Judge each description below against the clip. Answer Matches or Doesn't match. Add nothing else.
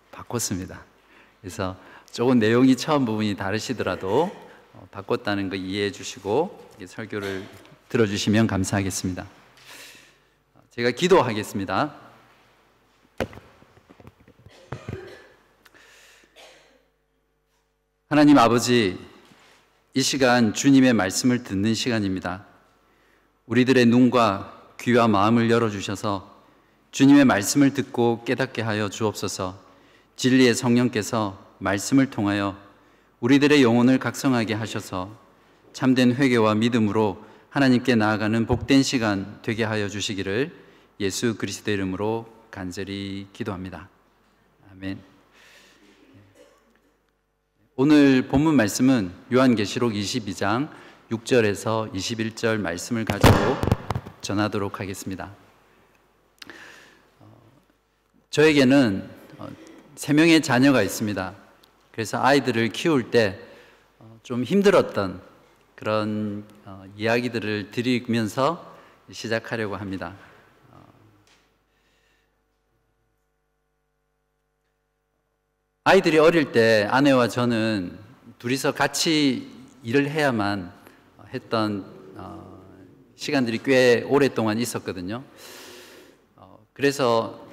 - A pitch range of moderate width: Matches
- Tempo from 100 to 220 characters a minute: Matches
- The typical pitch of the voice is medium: Doesn't match